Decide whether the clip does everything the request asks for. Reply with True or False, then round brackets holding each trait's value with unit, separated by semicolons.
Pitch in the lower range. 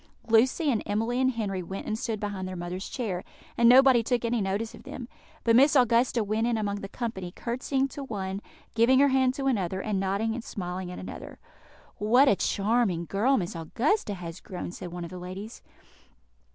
False (220 Hz)